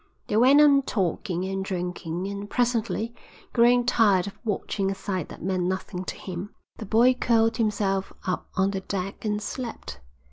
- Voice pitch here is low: No, high, 200 Hz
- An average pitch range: Yes, average, 3.5 semitones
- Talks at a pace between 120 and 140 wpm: No, average, 170 wpm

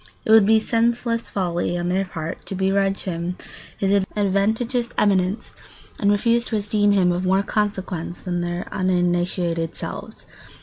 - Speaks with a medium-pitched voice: No, high, 195 Hz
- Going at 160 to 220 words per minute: No, average, 145 wpm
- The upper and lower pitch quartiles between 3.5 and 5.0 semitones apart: No, average, 3.0 semitones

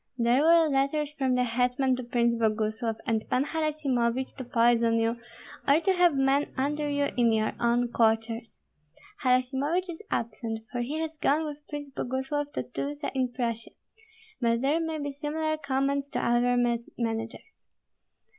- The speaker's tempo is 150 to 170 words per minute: Yes, average, 155 wpm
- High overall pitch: Yes, very high, 260 Hz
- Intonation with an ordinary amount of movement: Yes, average, 3.8 semitones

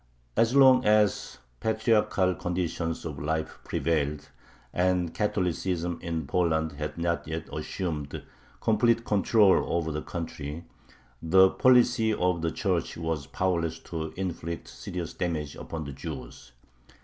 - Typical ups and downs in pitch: Yes, average, 3.1 semitones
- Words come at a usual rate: No, slow, 125 wpm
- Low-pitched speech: Yes, very low, 85 Hz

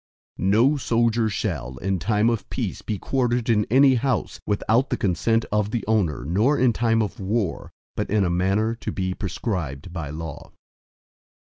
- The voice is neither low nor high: No, low, 105 Hz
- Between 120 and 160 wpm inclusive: No, average, 175 wpm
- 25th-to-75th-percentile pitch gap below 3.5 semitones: No, average, 4.0 semitones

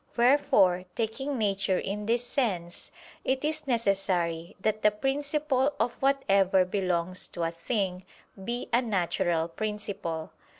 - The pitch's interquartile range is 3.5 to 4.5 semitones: No, wide, 5.4 semitones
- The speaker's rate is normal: No, slow, 125 wpm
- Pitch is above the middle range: Yes, high, 205 Hz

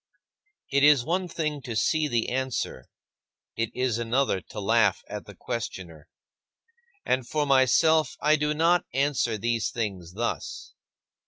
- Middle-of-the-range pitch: No, low, 130 Hz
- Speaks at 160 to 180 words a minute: No, average, 140 wpm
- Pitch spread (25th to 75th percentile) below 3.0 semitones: No, average, 4.7 semitones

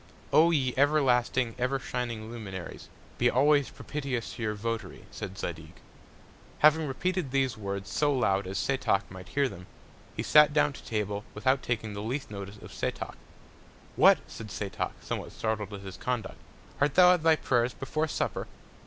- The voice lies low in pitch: Yes, low, 125 Hz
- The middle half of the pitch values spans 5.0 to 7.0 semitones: Yes, wide, 5.4 semitones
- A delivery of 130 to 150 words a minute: No, average, 165 wpm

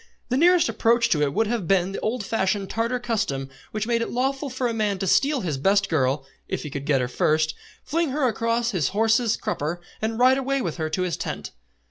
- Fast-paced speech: Yes, fast, 225 wpm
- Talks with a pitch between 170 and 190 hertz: No, high, 220 Hz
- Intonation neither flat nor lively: No, wide, 6.3 semitones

